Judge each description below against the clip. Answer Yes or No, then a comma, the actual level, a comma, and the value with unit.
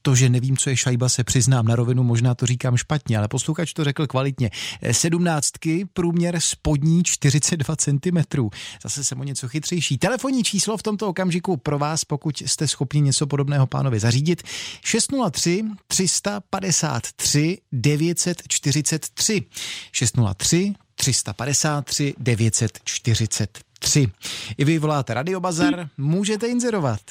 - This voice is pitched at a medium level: Yes, medium, 145 Hz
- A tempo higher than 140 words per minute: No, average, 125 wpm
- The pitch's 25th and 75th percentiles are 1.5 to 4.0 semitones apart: No, average, 5.2 semitones